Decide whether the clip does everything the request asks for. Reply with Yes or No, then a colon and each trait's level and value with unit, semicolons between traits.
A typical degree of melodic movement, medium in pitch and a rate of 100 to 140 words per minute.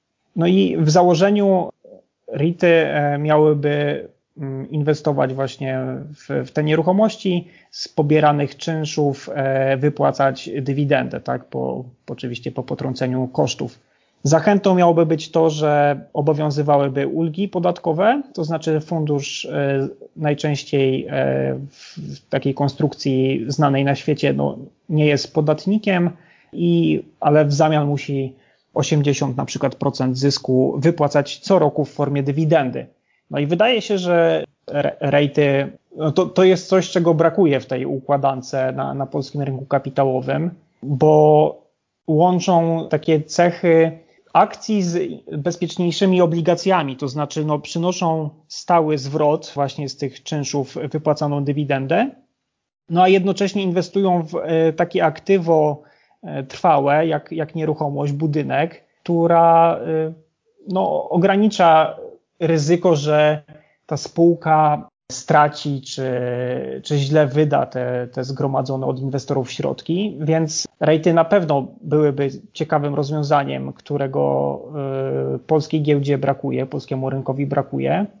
Yes: average, 3.1 semitones; medium, 150 Hz; average, 115 wpm